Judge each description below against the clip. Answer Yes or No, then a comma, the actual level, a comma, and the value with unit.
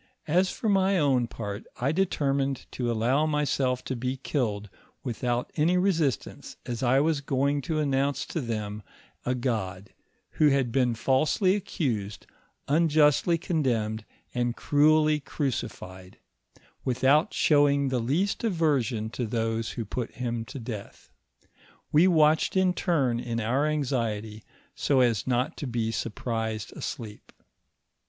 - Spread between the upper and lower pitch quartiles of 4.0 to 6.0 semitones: Yes, average, 4.6 semitones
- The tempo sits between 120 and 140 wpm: Yes, slow, 135 wpm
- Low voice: Yes, low, 130 Hz